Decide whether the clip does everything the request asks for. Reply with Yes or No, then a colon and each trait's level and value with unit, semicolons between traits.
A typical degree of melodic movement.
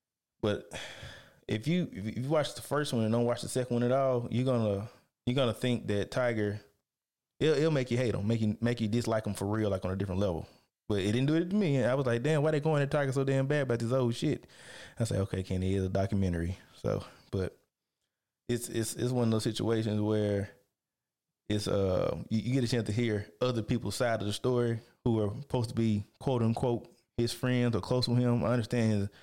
Yes: average, 3.1 semitones